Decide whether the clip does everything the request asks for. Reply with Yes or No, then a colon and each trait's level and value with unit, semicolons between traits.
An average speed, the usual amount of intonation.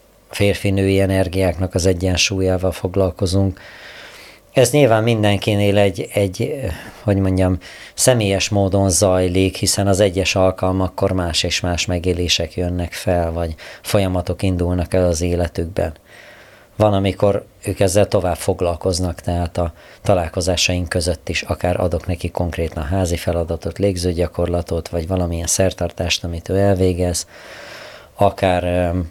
No: average, 120 wpm; narrow, 2.0 semitones